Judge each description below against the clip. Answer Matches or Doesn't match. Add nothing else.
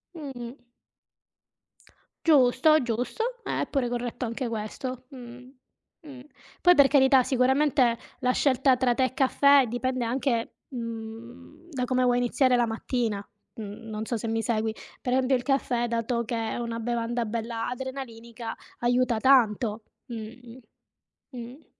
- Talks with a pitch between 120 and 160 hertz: Doesn't match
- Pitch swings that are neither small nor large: Doesn't match